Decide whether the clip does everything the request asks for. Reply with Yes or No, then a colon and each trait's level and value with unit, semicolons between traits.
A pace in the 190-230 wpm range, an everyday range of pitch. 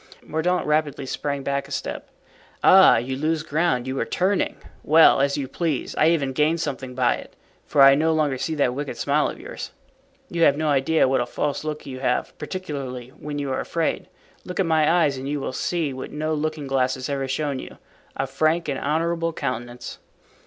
Yes: average, 200 wpm; average, 3.0 semitones